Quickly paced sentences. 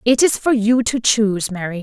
Yes: fast, 230 wpm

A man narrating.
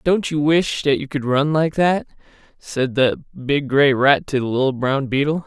Yes: male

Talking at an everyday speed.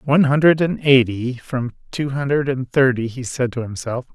Yes: average, 190 wpm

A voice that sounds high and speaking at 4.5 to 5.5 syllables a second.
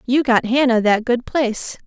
Yes: high, 245 Hz; 4.8 syllables/s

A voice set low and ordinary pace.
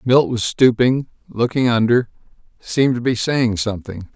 Yes: low, 120 Hz; average, 145 wpm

